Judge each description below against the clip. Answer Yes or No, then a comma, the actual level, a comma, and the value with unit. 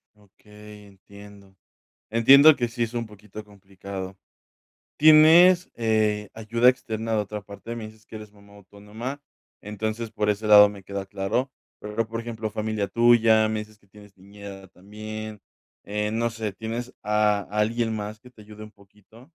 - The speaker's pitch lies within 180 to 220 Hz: No, low, 105 Hz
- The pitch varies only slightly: Yes, narrow, 1.9 semitones